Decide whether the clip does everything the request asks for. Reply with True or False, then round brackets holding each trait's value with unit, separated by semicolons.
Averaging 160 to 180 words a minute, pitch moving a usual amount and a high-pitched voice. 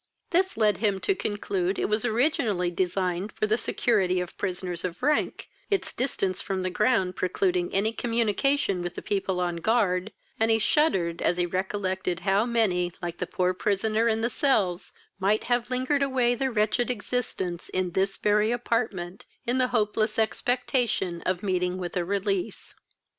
True (165 wpm; 4.3 semitones; 200 Hz)